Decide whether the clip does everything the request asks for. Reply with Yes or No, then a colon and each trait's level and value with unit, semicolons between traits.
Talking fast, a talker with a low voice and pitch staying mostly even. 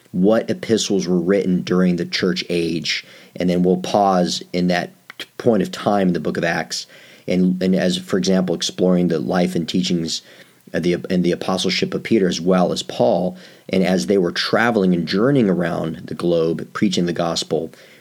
No: average, 185 wpm; very low, 90 Hz; narrow, 1.1 semitones